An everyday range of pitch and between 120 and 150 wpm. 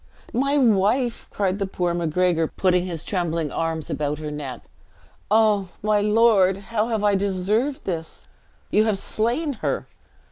Yes: average, 4.1 semitones; average, 145 wpm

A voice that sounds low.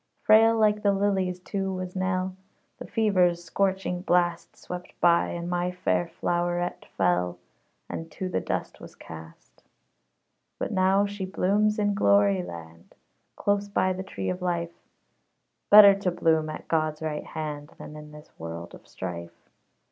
No: medium, 175 Hz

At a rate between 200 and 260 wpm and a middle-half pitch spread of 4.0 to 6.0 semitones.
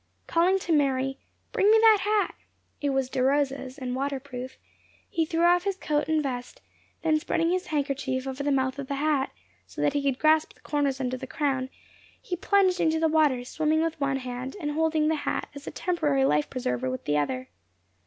No: fast, 205 wpm; average, 3.5 semitones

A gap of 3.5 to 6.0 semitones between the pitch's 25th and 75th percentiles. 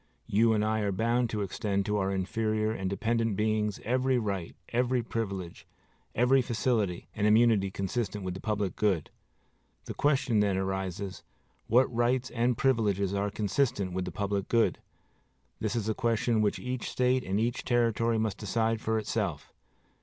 No: average, 3.0 semitones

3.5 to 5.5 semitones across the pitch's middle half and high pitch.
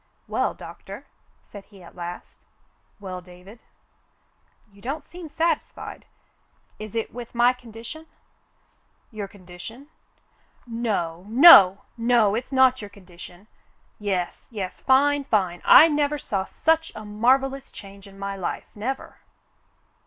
Yes: average, 5.2 semitones; high, 215 Hz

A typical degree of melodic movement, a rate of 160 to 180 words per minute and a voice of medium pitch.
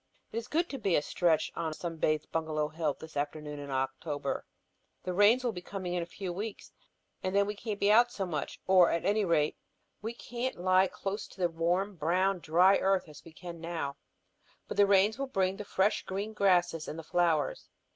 No: average, 3.8 semitones; fast, 205 wpm; medium, 180 Hz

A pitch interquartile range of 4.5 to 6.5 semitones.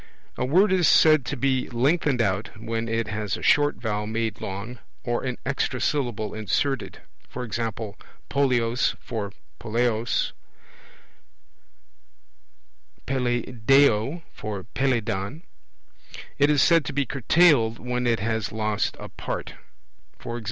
No: average, 3.7 semitones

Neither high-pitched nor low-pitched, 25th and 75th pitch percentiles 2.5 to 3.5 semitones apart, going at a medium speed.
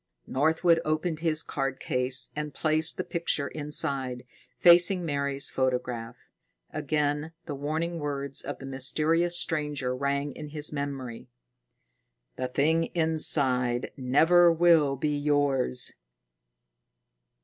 No: medium, 145 Hz; average, 2.9 semitones; slow, 110 wpm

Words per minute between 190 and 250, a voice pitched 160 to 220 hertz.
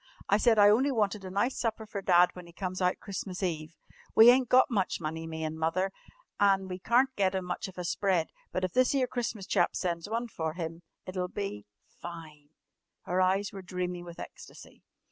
Yes: fast, 205 wpm; medium, 185 Hz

